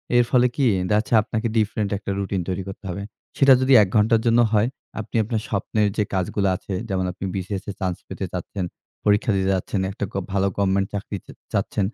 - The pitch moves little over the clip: Yes, narrow, 2.2 semitones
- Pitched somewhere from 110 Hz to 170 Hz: No, low, 100 Hz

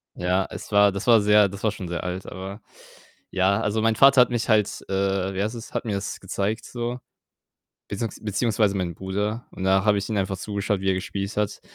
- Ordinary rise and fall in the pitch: No, narrow, 2.2 semitones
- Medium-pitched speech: No, low, 100 Hz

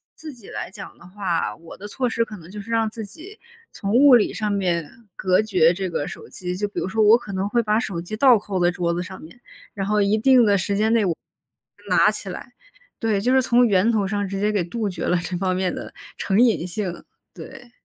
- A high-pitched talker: Yes, high, 205 Hz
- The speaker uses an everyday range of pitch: Yes, average, 3.6 semitones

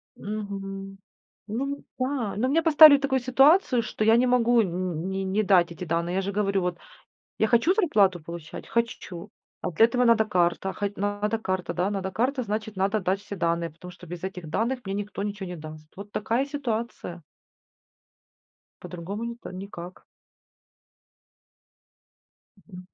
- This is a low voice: No, high, 200 Hz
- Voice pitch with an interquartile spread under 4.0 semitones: No, average, 4.3 semitones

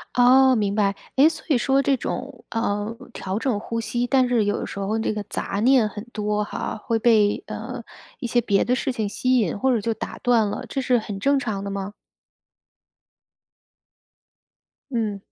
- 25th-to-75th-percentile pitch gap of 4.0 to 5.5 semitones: No, average, 3.4 semitones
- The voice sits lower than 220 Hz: No, high, 225 Hz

